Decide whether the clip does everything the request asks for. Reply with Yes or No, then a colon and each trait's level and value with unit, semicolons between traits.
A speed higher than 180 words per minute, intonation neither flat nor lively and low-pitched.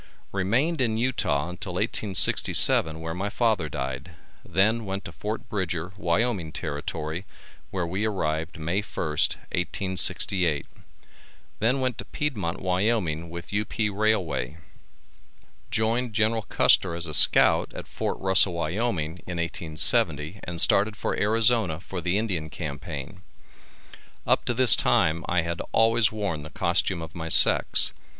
No: slow, 135 wpm; average, 4.9 semitones; very low, 95 Hz